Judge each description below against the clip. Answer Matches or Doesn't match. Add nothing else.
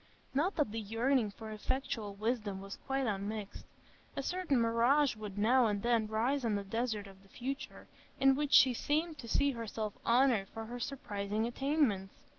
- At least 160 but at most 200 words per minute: Matches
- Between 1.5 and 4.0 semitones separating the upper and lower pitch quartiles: Doesn't match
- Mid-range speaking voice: Doesn't match